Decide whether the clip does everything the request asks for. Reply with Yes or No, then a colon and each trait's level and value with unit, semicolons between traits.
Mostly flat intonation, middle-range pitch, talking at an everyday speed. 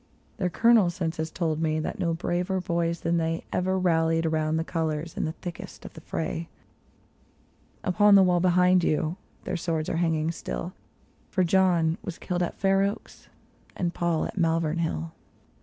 Yes: narrow, 2.1 semitones; medium, 170 Hz; average, 175 wpm